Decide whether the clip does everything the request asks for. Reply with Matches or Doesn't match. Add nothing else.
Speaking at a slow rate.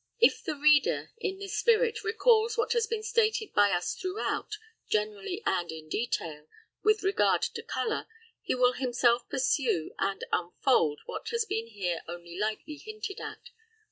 Doesn't match